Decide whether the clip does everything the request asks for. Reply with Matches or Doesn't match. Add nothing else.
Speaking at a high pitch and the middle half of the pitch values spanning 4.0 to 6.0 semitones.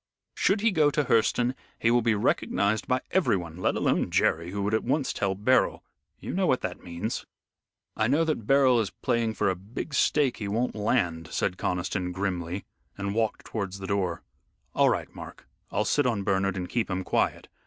Doesn't match